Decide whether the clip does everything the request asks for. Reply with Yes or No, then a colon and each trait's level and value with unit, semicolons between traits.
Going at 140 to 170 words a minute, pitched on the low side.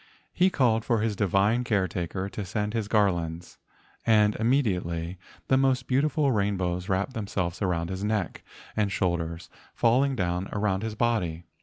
Yes: average, 155 wpm; low, 105 Hz